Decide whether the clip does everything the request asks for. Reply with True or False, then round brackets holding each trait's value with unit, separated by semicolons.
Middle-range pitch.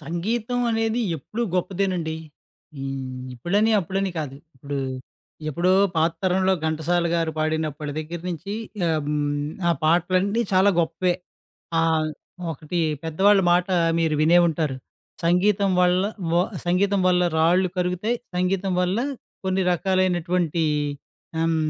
True (175 Hz)